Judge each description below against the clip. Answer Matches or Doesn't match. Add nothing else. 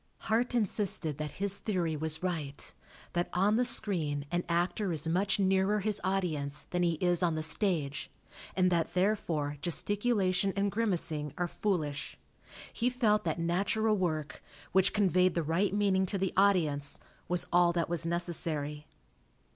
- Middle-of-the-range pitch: Matches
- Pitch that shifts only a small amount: Doesn't match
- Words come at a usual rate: Matches